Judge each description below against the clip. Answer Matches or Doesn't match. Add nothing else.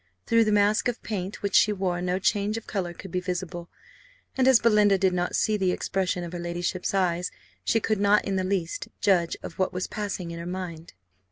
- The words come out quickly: Matches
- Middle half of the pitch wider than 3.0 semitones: Doesn't match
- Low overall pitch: Doesn't match